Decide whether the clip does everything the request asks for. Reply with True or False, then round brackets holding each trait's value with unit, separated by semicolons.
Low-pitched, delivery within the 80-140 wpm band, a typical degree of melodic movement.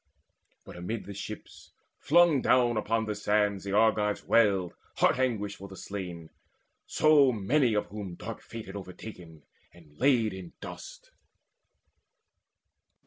True (105 Hz; 135 wpm; 3.4 semitones)